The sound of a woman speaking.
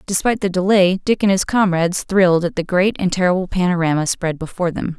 Yes: female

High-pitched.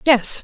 Yes: very high, 250 Hz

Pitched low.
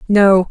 No: high, 195 Hz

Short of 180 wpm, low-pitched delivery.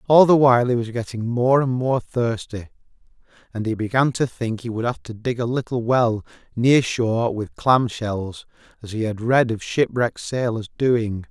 No: average, 190 wpm; low, 115 Hz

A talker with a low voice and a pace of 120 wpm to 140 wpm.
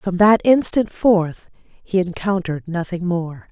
No: medium, 185 Hz; slow, 135 wpm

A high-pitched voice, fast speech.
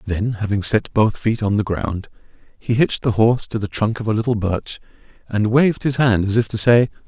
No: low, 110 Hz; fast, 230 wpm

